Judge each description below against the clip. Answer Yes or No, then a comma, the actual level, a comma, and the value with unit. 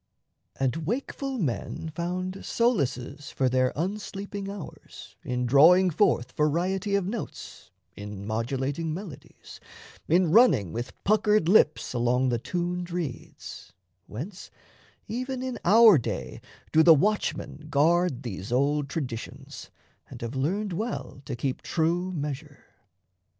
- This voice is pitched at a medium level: Yes, medium, 160 Hz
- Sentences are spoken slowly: Yes, slow, 120 wpm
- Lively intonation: Yes, wide, 6.8 semitones